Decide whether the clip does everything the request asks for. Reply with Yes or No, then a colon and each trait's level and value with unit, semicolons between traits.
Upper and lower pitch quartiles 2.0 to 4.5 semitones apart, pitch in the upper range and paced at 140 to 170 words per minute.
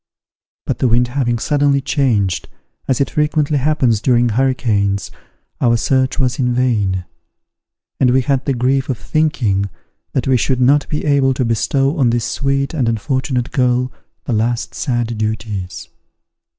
No: average, 2.9 semitones; low, 125 Hz; average, 150 wpm